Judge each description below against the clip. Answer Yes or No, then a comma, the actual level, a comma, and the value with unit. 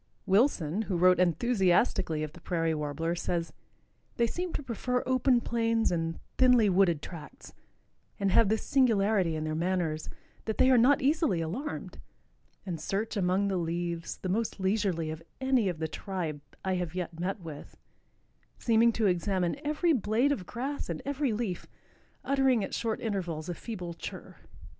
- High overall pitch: Yes, high, 195 Hz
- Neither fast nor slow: Yes, average, 160 wpm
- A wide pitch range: Yes, wide, 5.7 semitones